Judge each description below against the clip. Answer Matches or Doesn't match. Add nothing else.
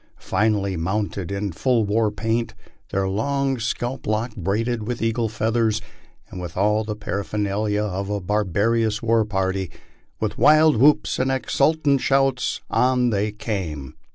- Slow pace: Doesn't match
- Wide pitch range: Doesn't match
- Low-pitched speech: Matches